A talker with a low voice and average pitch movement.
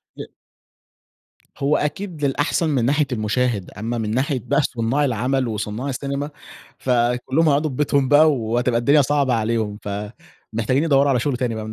Yes: low, 130 Hz; average, 3.7 semitones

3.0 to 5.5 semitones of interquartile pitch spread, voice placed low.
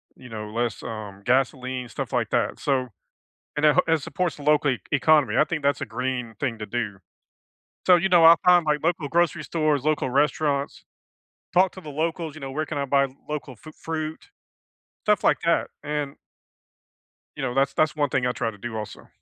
No: average, 3.8 semitones; medium, 145 Hz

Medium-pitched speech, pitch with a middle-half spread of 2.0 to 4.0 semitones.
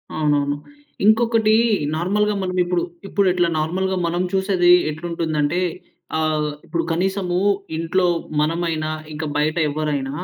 Yes: medium, 170 Hz; average, 3.3 semitones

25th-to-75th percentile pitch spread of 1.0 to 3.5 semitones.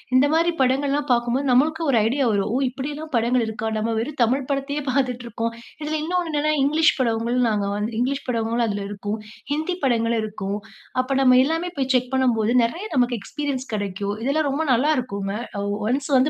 No: average, 3.9 semitones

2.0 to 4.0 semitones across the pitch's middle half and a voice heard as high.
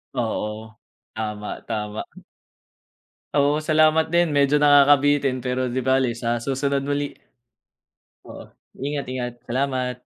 No: average, 3.2 semitones; low, 135 Hz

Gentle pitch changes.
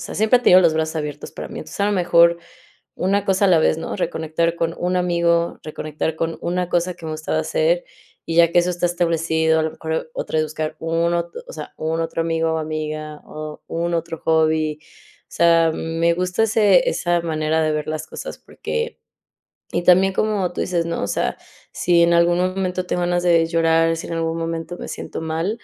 Yes: narrow, 1.8 semitones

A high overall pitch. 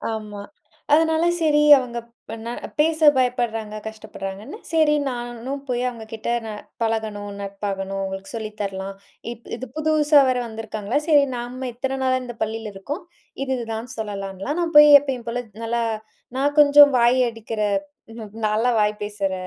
Yes: high, 235 Hz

